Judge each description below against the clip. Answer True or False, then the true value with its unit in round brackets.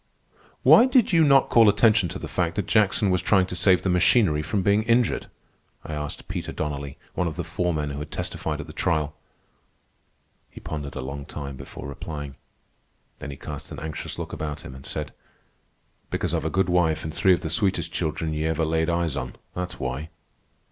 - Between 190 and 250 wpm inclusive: True (200 wpm)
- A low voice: True (80 Hz)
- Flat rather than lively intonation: False (4.1 semitones)